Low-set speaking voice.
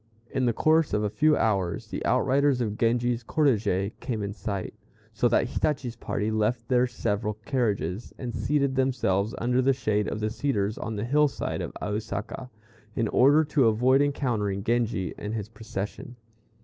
Yes: low, 115 Hz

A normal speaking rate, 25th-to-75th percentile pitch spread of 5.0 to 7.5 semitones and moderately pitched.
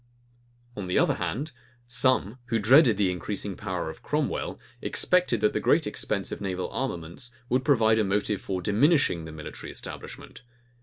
No: average, 160 wpm; wide, 5.5 semitones; low, 105 Hz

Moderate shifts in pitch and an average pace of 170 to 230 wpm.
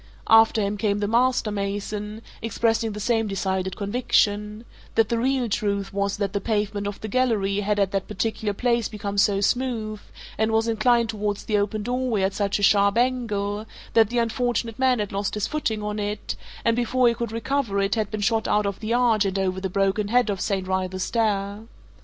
No: narrow, 2.3 semitones; average, 200 wpm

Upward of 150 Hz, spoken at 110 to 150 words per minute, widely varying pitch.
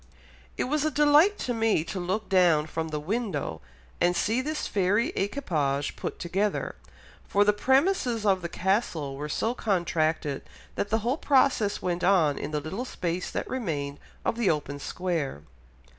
No: high, 190 Hz; average, 165 wpm; wide, 6.8 semitones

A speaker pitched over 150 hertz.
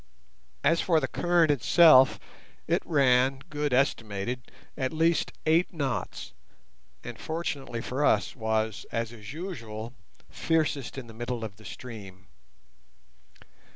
No: low, 130 Hz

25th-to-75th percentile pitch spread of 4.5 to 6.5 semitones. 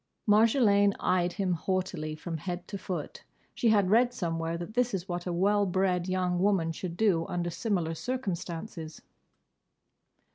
No: average, 3.1 semitones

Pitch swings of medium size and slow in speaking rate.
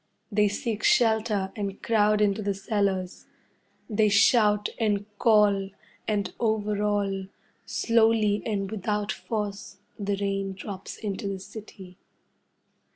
No: narrow, 1.5 semitones; slow, 115 wpm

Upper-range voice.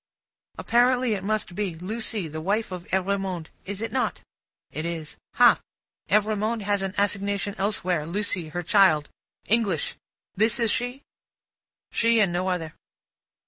Yes: high, 200 Hz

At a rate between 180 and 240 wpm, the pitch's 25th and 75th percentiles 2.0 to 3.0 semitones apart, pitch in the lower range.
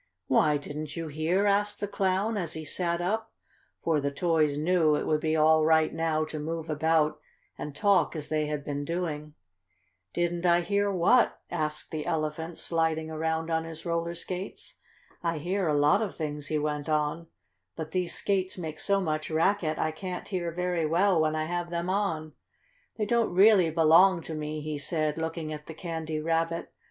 No: average, 185 wpm; narrow, 2.4 semitones; medium, 160 Hz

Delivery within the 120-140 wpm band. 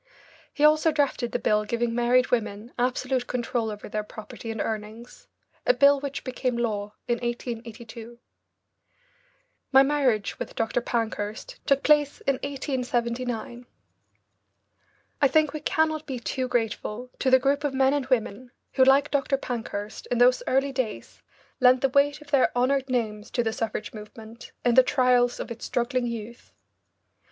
No: average, 155 wpm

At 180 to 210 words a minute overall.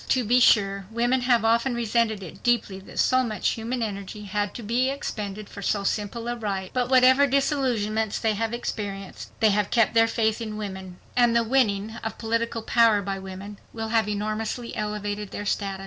Yes: average, 190 wpm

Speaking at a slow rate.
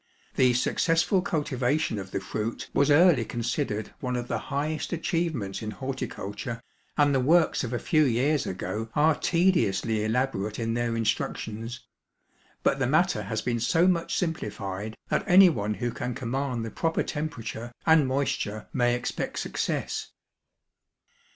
No: average, 145 wpm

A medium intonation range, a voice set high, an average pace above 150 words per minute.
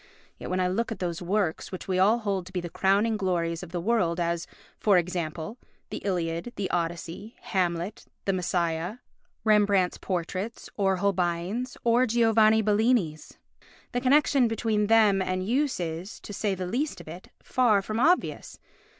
Yes: average, 4.1 semitones; high, 195 Hz; average, 165 wpm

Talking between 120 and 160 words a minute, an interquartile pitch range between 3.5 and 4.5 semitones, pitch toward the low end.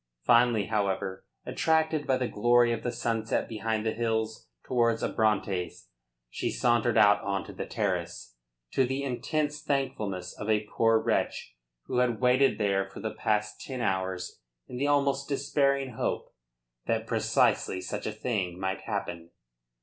Yes: average, 150 wpm; average, 3.9 semitones; low, 115 Hz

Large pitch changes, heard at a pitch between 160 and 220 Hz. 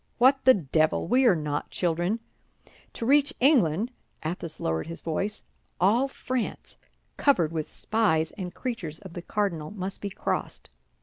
Yes: wide, 6.8 semitones; high, 190 Hz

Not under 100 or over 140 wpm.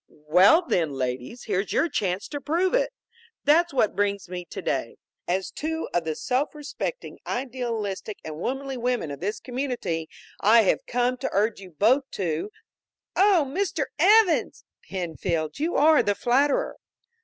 No: average, 155 wpm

